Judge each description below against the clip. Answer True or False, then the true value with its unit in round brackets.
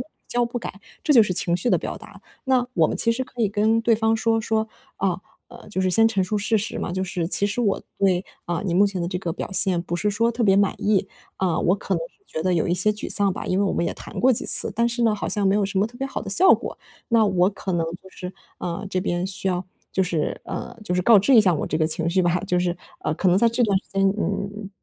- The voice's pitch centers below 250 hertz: True (195 Hz)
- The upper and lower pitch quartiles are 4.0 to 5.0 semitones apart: False (3.6 semitones)